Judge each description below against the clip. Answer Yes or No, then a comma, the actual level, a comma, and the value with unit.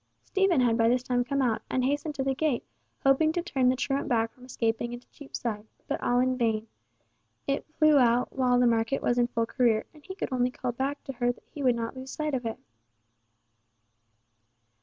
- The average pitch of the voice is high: Yes, very high, 250 Hz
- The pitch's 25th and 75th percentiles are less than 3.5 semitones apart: Yes, narrow, 2.5 semitones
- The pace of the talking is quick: Yes, fast, 210 wpm